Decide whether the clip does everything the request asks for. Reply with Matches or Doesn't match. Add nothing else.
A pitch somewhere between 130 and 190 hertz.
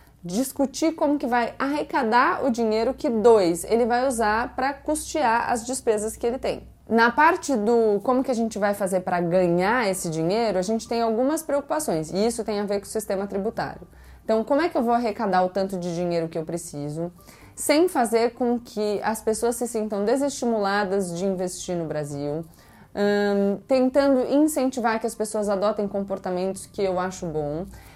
Doesn't match